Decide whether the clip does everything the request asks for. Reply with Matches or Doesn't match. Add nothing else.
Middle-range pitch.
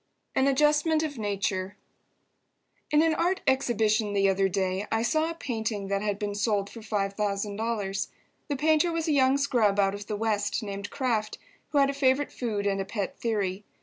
Doesn't match